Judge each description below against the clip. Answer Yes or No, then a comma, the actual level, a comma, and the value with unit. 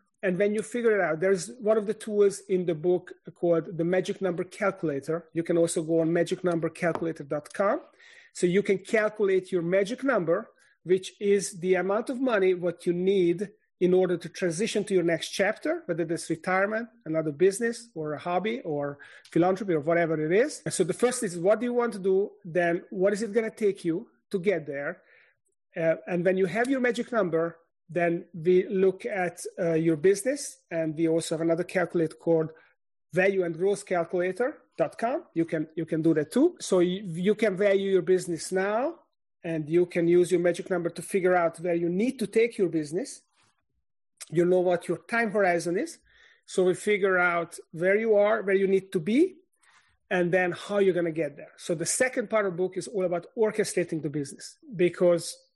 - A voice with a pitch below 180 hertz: No, medium, 185 Hz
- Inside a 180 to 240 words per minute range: Yes, average, 195 wpm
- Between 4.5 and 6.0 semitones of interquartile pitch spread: No, average, 3.5 semitones